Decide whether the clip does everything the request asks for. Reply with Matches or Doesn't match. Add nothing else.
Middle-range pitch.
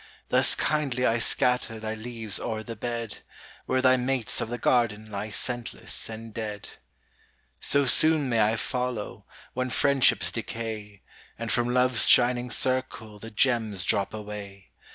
Doesn't match